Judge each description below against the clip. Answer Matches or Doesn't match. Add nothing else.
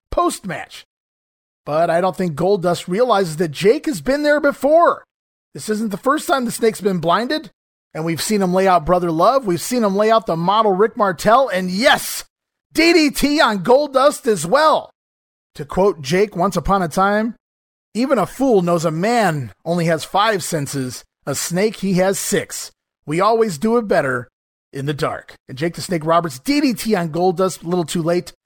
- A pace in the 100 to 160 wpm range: Doesn't match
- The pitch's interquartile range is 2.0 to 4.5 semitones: Doesn't match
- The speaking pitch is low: Doesn't match